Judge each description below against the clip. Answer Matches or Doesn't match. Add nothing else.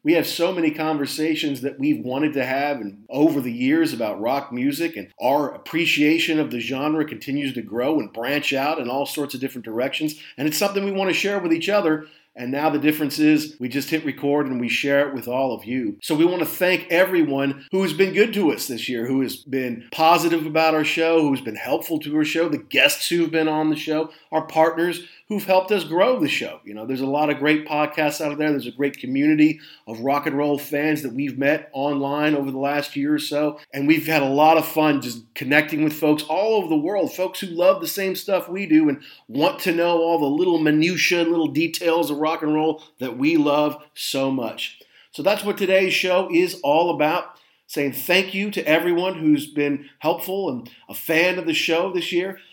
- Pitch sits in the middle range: Matches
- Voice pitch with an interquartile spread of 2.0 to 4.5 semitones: Matches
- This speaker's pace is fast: Matches